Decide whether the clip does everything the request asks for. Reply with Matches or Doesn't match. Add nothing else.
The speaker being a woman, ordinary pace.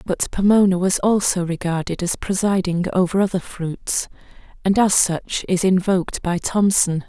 Matches